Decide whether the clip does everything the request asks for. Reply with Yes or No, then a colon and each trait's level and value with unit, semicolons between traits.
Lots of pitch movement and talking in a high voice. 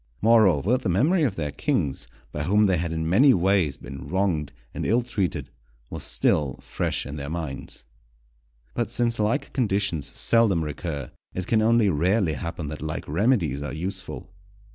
No: wide, 6.5 semitones; very low, 90 Hz